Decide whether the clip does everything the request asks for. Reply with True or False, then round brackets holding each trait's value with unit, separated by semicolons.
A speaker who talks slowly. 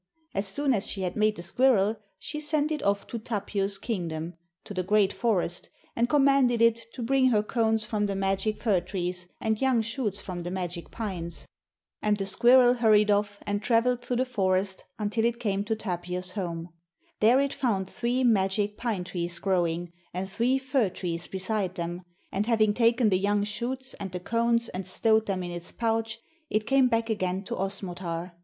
False (190 wpm)